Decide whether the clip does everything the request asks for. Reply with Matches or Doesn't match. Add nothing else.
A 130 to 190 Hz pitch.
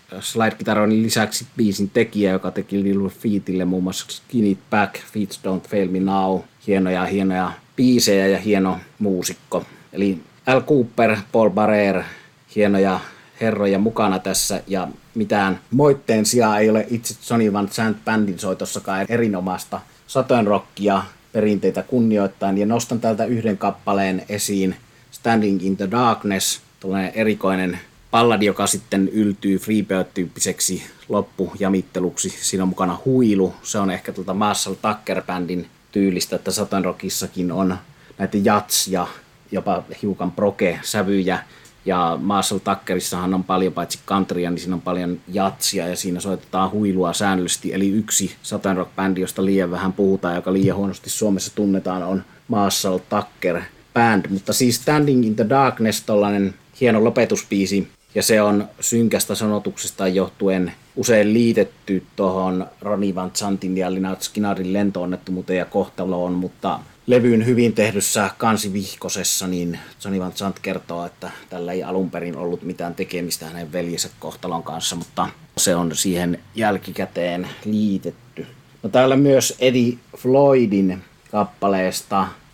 Doesn't match